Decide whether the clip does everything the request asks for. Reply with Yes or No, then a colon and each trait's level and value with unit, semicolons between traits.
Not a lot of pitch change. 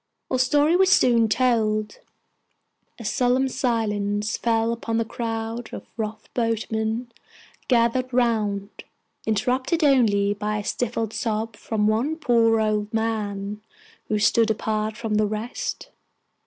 Yes: narrow, 2.2 semitones